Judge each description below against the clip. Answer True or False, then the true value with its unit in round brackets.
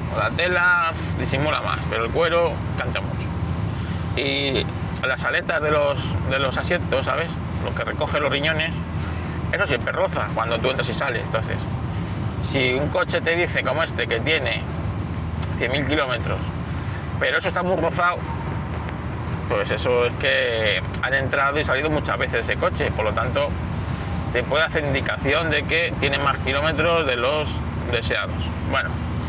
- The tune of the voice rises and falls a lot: True (8.7 semitones)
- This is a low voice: True (115 Hz)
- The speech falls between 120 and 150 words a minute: False (160 wpm)